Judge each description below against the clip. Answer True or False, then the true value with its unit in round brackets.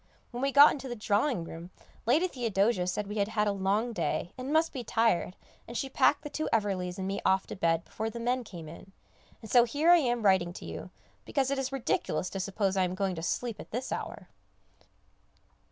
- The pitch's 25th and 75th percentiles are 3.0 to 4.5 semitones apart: False (5.1 semitones)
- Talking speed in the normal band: False (220 wpm)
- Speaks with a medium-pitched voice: False (220 Hz)